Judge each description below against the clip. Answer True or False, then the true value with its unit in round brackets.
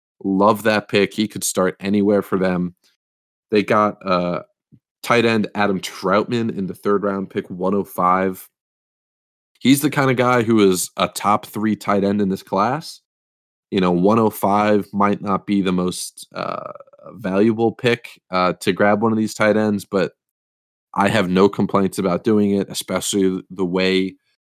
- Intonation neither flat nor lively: False (2.2 semitones)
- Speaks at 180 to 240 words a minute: False (165 wpm)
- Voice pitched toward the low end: True (100 Hz)